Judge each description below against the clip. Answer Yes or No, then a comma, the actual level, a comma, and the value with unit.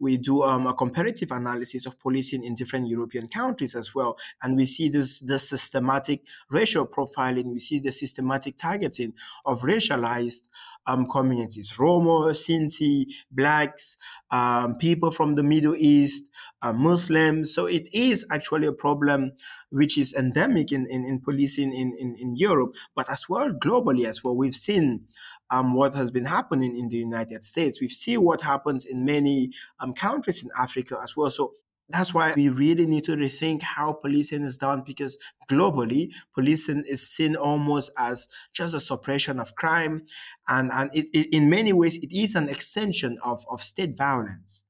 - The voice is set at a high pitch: No, medium, 140 Hz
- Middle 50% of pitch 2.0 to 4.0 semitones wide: Yes, average, 3.2 semitones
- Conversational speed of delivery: Yes, average, 170 wpm